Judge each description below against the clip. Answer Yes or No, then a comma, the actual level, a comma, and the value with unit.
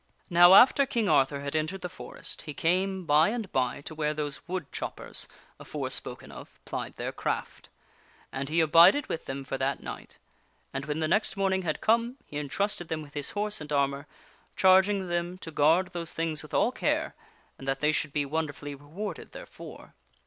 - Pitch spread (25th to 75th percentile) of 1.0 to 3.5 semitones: No, average, 4.5 semitones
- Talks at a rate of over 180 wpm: Yes, average, 200 wpm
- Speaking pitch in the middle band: Yes, medium, 160 Hz